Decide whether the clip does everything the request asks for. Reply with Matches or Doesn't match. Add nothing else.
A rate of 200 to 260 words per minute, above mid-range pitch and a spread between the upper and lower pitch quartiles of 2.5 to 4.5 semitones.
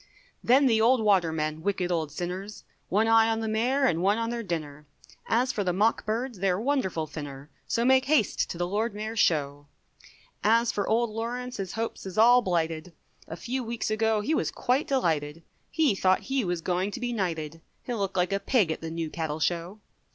Doesn't match